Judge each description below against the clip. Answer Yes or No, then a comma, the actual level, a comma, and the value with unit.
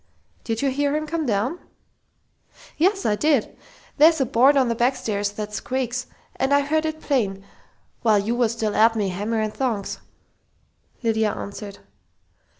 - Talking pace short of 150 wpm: No, average, 155 wpm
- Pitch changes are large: No, average, 5.0 semitones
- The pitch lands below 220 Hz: No, high, 235 Hz